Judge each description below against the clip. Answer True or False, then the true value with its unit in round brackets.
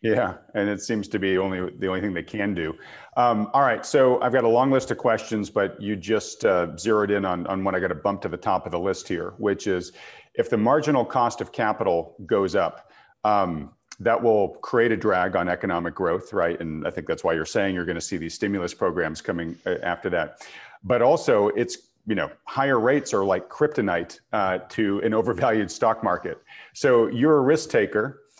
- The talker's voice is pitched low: True (100 Hz)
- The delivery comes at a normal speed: False (215 wpm)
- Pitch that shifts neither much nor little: True (3.8 semitones)